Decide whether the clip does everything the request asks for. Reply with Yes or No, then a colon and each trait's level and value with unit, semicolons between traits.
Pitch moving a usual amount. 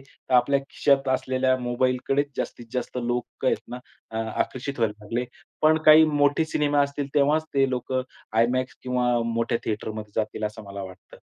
Yes: average, 3.1 semitones